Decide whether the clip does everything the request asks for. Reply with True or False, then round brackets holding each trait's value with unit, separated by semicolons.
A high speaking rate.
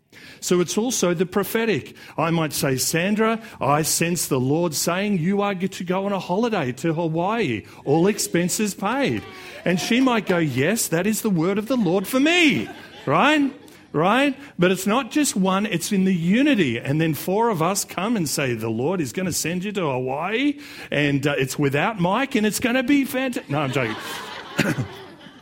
False (195 wpm)